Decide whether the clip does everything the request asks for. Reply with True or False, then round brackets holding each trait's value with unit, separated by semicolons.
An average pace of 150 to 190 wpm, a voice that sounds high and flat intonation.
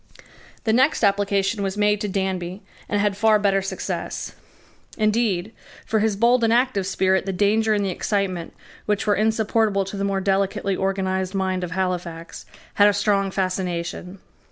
True (160 wpm; 200 Hz; 1.8 semitones)